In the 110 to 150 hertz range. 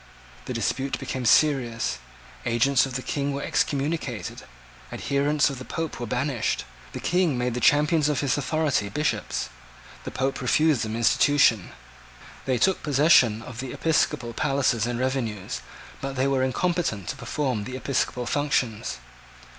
Yes: low, 135 Hz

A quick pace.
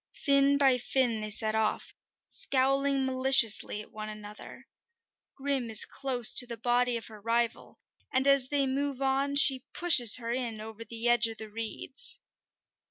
No: average, 165 wpm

